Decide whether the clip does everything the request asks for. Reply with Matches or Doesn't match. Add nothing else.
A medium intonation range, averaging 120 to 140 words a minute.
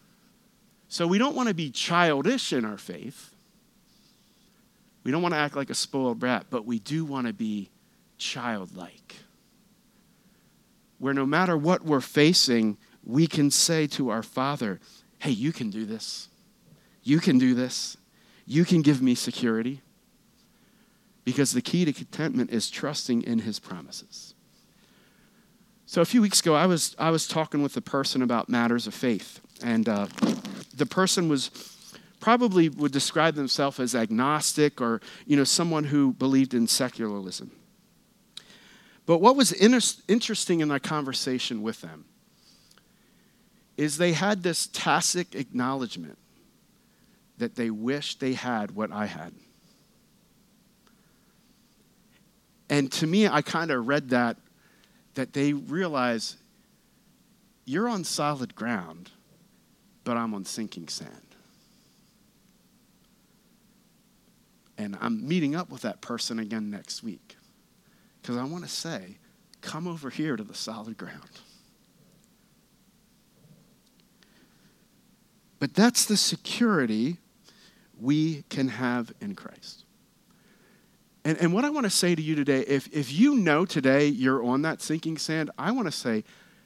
Doesn't match